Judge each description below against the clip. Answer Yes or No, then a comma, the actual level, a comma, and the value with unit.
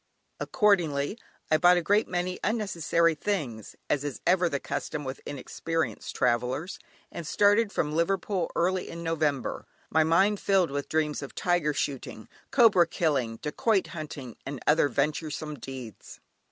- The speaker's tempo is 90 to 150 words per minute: Yes, average, 140 wpm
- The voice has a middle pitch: Yes, medium, 160 Hz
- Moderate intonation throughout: Yes, average, 4.2 semitones